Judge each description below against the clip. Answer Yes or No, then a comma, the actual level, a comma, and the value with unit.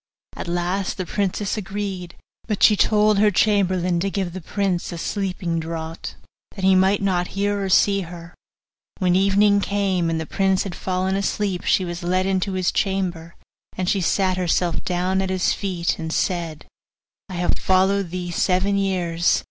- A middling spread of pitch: No, narrow, 2.0 semitones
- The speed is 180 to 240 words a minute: No, average, 170 wpm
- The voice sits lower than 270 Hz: Yes, medium, 185 Hz